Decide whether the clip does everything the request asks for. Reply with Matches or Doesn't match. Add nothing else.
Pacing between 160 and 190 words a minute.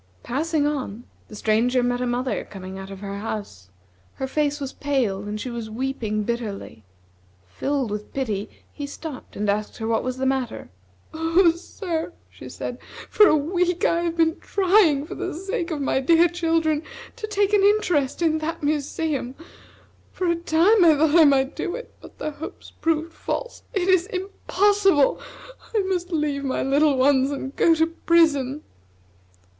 Matches